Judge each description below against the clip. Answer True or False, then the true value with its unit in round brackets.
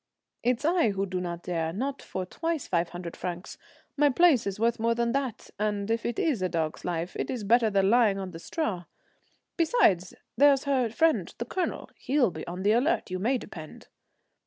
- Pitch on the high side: True (215 Hz)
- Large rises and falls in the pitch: True (6.7 semitones)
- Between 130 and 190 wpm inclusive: False (200 wpm)